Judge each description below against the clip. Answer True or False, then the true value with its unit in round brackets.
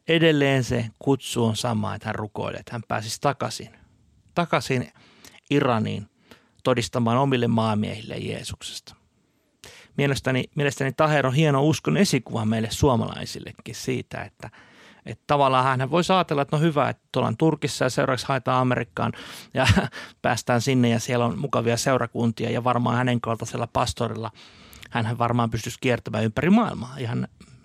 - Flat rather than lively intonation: False (3.3 semitones)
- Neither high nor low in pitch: False (125 Hz)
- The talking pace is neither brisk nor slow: True (140 wpm)